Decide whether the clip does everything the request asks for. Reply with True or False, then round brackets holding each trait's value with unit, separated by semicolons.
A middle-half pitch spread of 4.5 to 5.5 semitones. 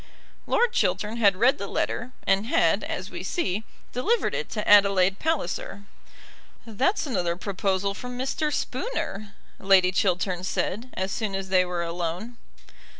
True (4.9 semitones)